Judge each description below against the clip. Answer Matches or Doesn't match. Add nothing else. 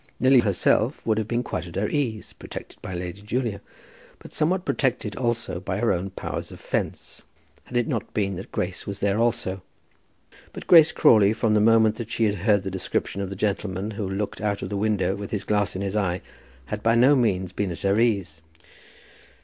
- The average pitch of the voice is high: Doesn't match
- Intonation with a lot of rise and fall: Doesn't match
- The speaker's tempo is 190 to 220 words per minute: Matches